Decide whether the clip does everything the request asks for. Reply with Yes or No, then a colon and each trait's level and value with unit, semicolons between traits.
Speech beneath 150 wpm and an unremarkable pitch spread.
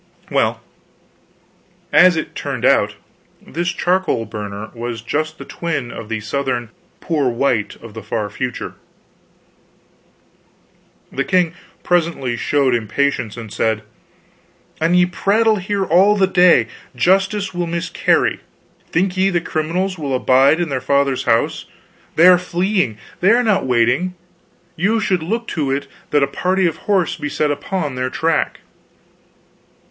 No: average, 140 wpm; wide, 6.4 semitones